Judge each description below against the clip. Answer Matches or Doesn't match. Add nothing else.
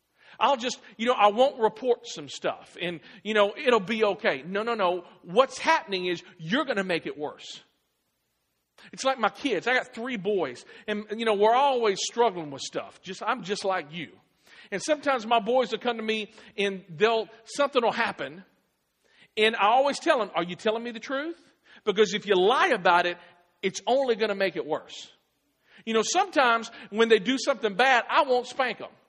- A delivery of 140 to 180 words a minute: Doesn't match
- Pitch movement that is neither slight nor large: Matches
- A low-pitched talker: Doesn't match